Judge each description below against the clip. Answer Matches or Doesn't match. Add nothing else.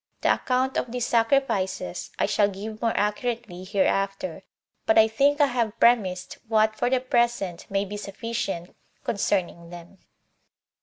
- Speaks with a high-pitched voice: Matches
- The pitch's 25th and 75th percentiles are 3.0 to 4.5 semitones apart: Matches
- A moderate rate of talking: Matches